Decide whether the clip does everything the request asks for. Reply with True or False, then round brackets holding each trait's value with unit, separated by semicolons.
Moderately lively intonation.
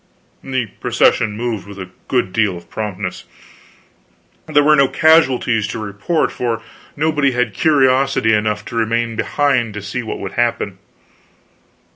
True (4.1 semitones)